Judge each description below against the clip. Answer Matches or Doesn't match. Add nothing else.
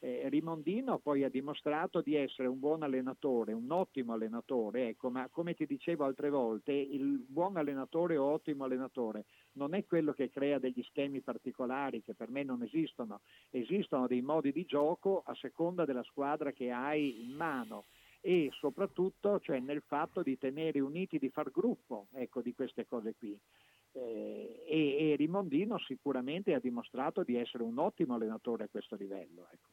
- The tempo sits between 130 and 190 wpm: Matches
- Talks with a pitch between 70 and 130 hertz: Doesn't match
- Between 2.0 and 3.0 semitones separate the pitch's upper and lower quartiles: Doesn't match